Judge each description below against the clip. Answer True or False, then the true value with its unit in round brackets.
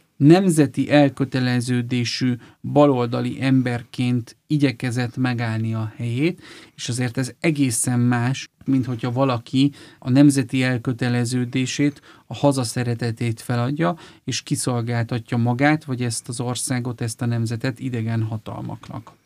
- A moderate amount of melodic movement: False (2.2 semitones)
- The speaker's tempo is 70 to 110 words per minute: True (105 wpm)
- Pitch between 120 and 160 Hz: True (125 Hz)